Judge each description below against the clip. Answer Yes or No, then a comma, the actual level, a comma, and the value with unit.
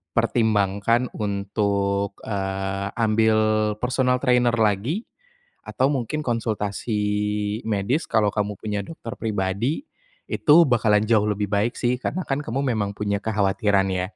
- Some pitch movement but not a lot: Yes, average, 3.0 semitones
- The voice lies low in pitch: Yes, low, 105 Hz